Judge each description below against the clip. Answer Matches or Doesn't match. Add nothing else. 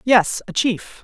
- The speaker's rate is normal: Matches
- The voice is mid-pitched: Doesn't match